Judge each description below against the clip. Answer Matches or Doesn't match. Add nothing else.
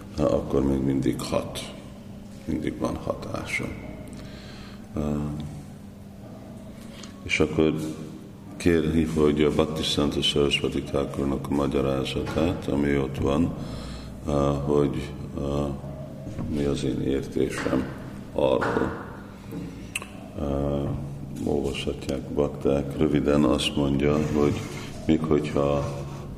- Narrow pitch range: Matches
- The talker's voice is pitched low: Matches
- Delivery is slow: Matches